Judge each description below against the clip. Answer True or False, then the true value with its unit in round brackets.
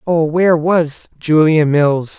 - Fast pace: False (135 wpm)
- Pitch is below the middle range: False (160 Hz)